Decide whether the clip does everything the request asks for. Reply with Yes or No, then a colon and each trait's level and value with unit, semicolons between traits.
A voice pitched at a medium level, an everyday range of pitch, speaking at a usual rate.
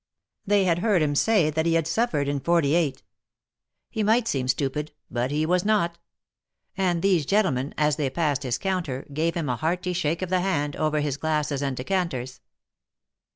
Yes: medium, 155 Hz; average, 4.1 semitones; average, 180 wpm